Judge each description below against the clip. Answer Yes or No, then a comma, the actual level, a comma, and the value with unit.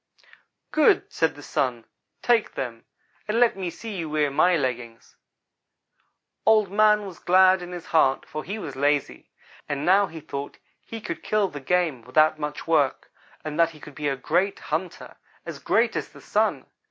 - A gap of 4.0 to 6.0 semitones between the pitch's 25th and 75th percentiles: Yes, average, 5.0 semitones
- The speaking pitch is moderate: Yes, medium, 160 Hz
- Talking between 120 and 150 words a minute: No, average, 175 wpm